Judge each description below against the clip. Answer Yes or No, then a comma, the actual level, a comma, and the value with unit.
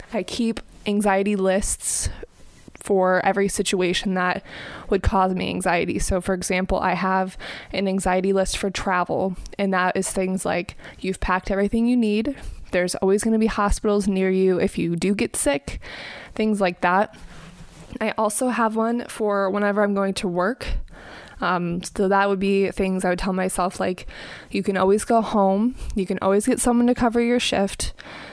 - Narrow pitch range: Yes, narrow, 2.1 semitones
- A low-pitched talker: No, high, 195 Hz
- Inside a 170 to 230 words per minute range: Yes, average, 175 wpm